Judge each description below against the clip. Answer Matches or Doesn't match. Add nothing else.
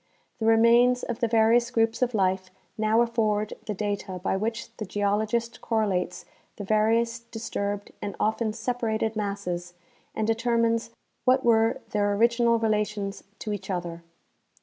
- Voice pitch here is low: Doesn't match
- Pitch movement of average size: Doesn't match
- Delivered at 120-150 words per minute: Matches